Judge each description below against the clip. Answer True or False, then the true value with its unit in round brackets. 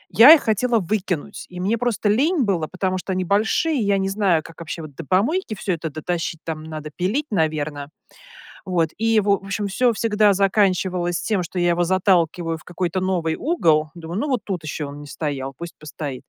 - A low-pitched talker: False (185 Hz)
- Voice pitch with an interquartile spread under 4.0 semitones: False (4.3 semitones)